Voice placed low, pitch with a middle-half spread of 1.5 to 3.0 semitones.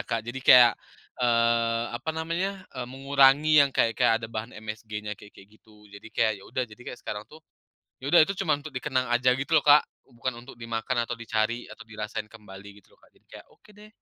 No: low, 120 Hz; average, 3.8 semitones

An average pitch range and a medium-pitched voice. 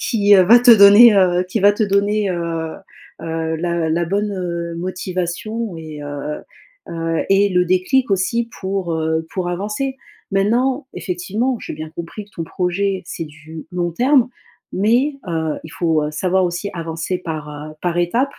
Yes: average, 3.8 semitones; medium, 180 Hz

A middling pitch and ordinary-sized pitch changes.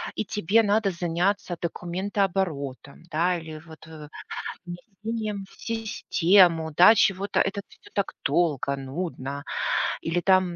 Yes: medium, 175 Hz; average, 3.8 semitones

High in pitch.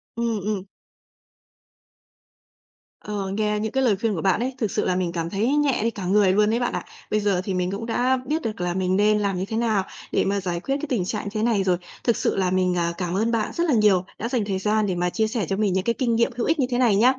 Yes: high, 210 Hz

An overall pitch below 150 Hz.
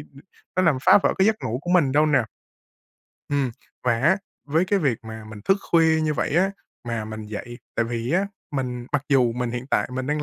Yes: low, 135 Hz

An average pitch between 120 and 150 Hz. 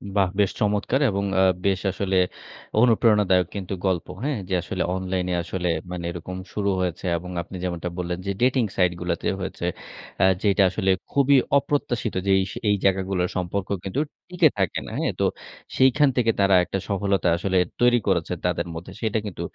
No: very low, 95 Hz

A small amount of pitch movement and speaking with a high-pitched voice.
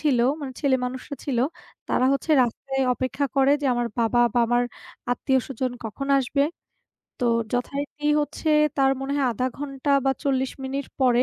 Yes: narrow, 2.1 semitones; very high, 270 Hz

